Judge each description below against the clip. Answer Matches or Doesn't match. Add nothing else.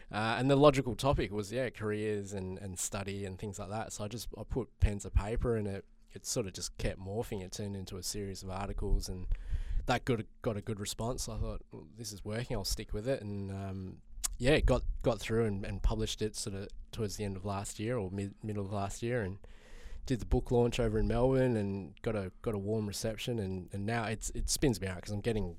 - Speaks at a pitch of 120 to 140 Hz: Doesn't match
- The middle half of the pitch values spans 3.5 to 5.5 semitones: Doesn't match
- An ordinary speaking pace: Doesn't match